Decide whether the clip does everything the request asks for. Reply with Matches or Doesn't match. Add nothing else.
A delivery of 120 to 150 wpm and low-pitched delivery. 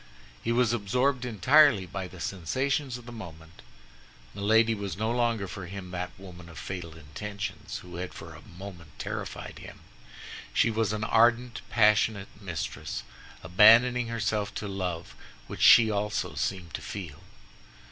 Matches